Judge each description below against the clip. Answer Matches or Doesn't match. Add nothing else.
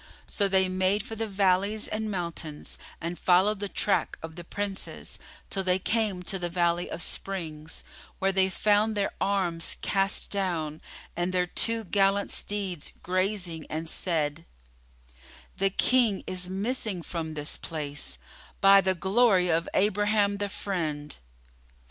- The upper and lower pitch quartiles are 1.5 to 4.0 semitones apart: Matches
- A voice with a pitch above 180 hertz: Matches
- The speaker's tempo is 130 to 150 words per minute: Matches